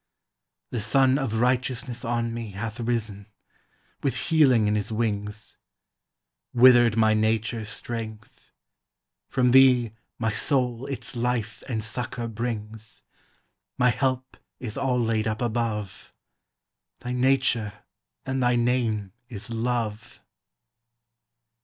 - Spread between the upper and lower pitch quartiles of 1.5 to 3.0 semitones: Yes, narrow, 2.4 semitones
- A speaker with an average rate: No, slow, 110 wpm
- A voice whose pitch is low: Yes, low, 115 Hz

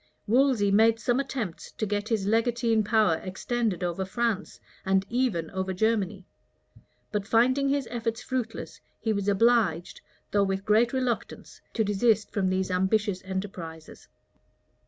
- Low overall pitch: No, high, 210 Hz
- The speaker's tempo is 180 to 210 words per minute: No, slow, 135 wpm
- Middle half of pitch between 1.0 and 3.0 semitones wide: No, average, 3.6 semitones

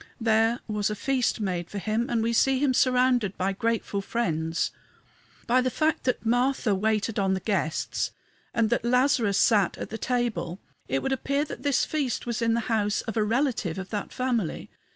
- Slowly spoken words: No, average, 190 wpm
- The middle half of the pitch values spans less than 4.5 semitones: Yes, average, 3.7 semitones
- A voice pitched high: Yes, high, 225 Hz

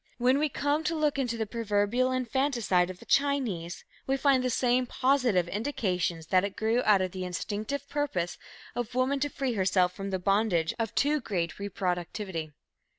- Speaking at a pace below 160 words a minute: No, average, 175 wpm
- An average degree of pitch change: No, wide, 6.2 semitones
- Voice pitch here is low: No, high, 225 Hz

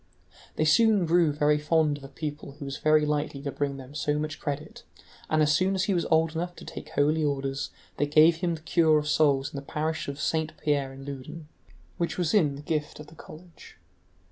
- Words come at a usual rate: No, fast, 220 wpm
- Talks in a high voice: No, medium, 150 Hz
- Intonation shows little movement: Yes, narrow, 1.9 semitones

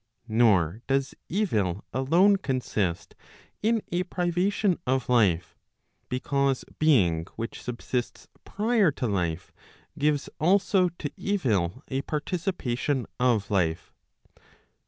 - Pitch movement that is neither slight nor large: No, wide, 9.0 semitones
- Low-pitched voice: Yes, low, 130 Hz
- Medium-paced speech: No, slow, 100 wpm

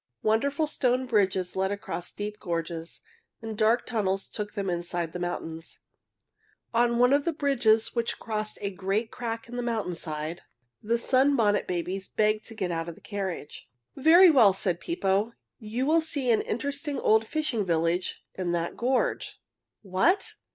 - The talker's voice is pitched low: No, high, 215 Hz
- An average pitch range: Yes, average, 4.8 semitones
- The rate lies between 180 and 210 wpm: No, average, 160 wpm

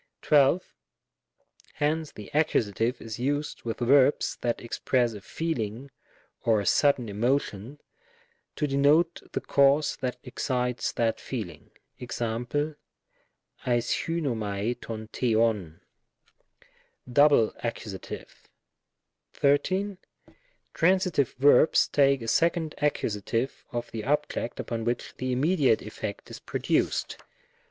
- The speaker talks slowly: Yes, slow, 110 wpm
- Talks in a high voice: No, low, 125 Hz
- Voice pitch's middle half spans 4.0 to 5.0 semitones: Yes, average, 4.4 semitones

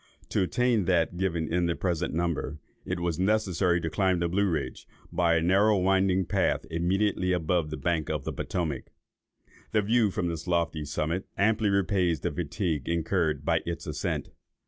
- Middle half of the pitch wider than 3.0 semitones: No, narrow, 2.6 semitones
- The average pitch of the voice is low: Yes, very low, 85 Hz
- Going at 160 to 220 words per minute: Yes, average, 170 wpm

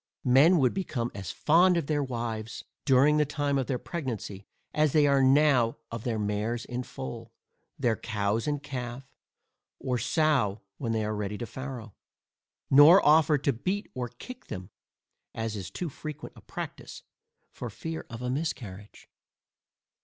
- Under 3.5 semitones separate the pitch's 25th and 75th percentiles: No, average, 4.8 semitones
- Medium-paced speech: Yes, average, 160 wpm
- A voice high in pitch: No, low, 130 Hz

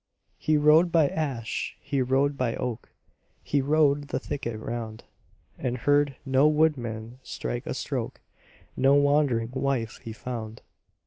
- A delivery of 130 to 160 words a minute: Yes, slow, 135 wpm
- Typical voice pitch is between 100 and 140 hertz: Yes, low, 135 Hz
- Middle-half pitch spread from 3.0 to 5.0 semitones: Yes, average, 3.8 semitones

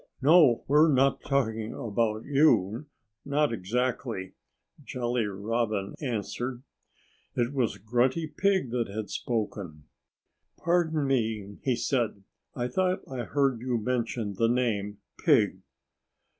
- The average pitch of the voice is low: Yes, low, 120 Hz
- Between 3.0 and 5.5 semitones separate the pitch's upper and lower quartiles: Yes, average, 4.0 semitones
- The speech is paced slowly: Yes, slow, 115 wpm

